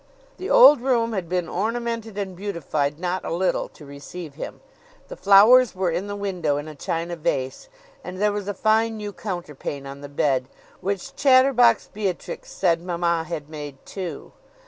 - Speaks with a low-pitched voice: No, medium, 185 Hz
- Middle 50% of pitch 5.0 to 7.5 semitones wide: Yes, average, 5.3 semitones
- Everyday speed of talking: Yes, average, 170 wpm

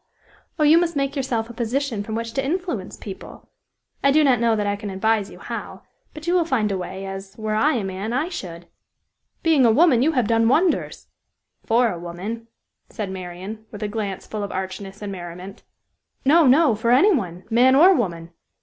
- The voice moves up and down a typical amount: No, wide, 5.9 semitones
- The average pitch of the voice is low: No, high, 225 Hz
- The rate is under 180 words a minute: No, fast, 205 wpm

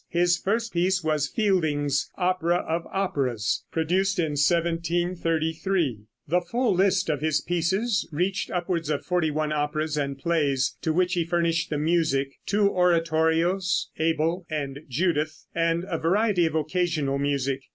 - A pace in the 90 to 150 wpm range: Yes, average, 140 wpm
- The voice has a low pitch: No, medium, 165 Hz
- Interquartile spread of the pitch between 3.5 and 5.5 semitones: No, average, 2.9 semitones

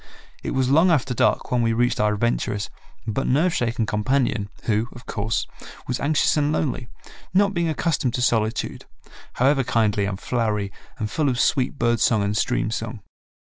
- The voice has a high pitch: No, low, 120 Hz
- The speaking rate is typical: Yes, average, 175 wpm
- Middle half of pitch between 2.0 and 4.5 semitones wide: Yes, average, 3.9 semitones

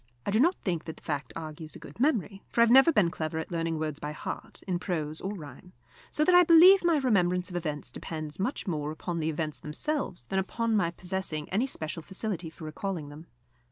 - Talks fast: Yes, fast, 225 wpm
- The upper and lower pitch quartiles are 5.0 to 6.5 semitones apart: Yes, wide, 5.6 semitones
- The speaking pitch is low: No, medium, 175 Hz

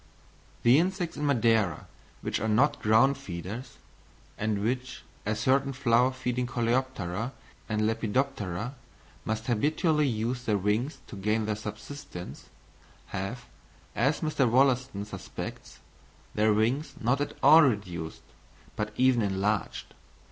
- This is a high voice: No, low, 115 Hz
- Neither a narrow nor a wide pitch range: Yes, average, 3.9 semitones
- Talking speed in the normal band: No, slow, 120 wpm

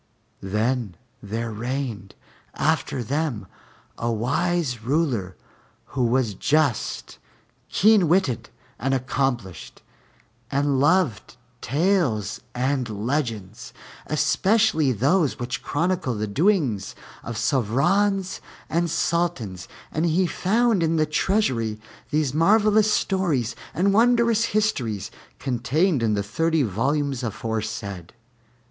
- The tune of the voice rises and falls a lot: Yes, wide, 7.2 semitones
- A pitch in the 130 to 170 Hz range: Yes, medium, 140 Hz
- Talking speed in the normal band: No, slow, 100 wpm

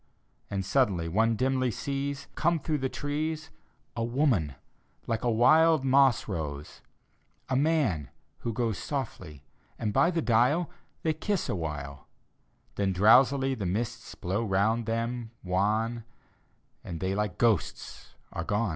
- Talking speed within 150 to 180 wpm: No, average, 140 wpm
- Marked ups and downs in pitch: Yes, wide, 6.0 semitones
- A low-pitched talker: Yes, low, 115 Hz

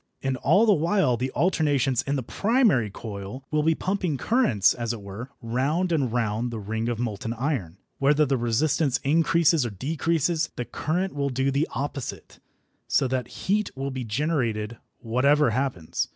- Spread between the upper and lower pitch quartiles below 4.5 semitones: No, average, 5.0 semitones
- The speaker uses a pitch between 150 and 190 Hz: No, low, 135 Hz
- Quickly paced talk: No, average, 165 wpm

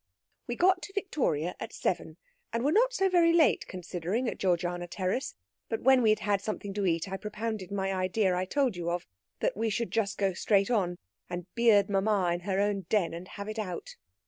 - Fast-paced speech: Yes, fast, 210 wpm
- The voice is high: Yes, high, 200 Hz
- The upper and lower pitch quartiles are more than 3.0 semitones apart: Yes, average, 4.0 semitones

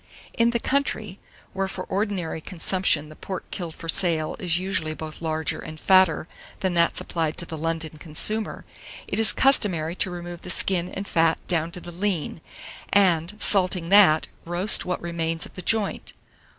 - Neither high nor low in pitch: Yes, medium, 175 Hz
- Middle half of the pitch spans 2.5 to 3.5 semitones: Yes, average, 2.9 semitones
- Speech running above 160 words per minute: Yes, average, 175 wpm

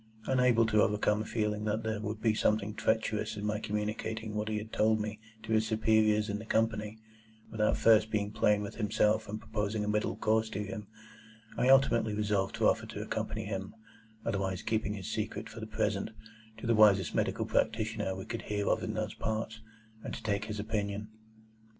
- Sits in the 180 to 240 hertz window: No, low, 110 Hz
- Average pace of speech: Yes, average, 195 wpm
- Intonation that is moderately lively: No, narrow, 1.0 semitones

